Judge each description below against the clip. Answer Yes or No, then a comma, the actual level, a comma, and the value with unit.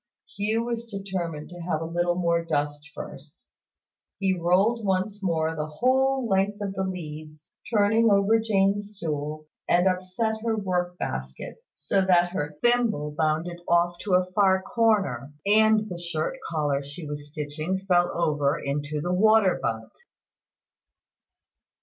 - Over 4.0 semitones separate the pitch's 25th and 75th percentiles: Yes, average, 4.8 semitones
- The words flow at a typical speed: Yes, average, 145 wpm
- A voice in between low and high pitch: Yes, medium, 180 Hz